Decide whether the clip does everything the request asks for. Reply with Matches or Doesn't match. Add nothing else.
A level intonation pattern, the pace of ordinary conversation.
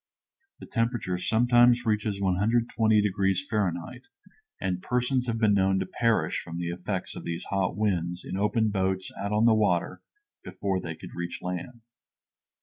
Doesn't match